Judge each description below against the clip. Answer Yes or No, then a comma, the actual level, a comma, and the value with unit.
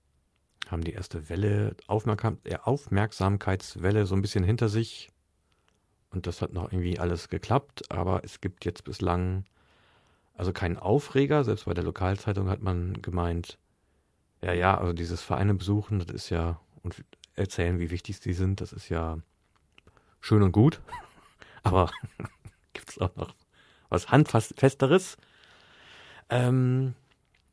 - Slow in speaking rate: No, average, 135 wpm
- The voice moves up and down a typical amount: Yes, average, 3.6 semitones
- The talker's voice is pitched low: Yes, very low, 95 Hz